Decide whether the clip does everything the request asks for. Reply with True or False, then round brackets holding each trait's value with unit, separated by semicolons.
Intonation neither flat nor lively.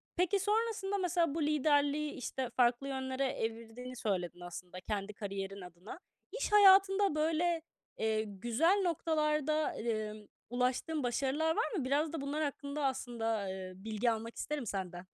False (6.4 semitones)